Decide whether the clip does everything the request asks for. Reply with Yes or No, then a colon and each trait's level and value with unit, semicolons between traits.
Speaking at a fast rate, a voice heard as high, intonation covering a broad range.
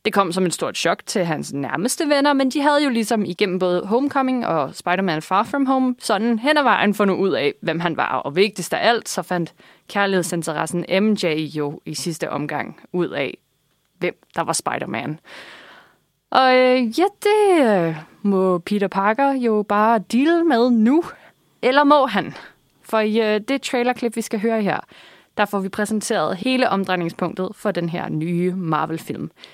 No: average, 175 wpm; high, 205 Hz; wide, 5.9 semitones